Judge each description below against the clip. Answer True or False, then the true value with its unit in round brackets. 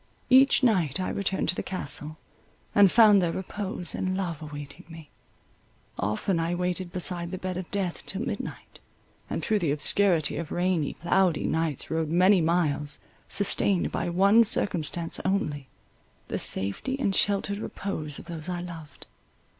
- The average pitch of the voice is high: False (180 Hz)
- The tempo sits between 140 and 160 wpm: True (155 wpm)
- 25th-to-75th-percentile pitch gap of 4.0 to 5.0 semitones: False (3.5 semitones)